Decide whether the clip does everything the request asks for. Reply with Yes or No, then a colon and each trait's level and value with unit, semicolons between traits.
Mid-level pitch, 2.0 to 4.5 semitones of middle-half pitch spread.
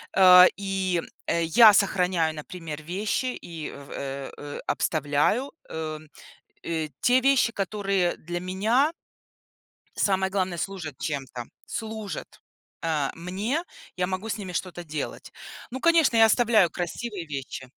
No: medium, 180 Hz; average, 5.0 semitones